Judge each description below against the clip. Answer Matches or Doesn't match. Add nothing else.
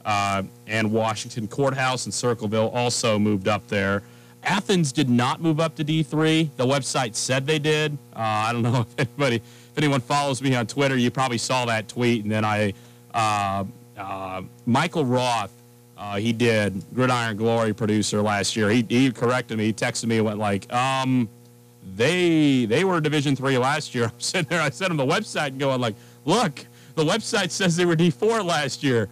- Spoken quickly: Doesn't match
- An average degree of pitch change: Matches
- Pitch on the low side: Matches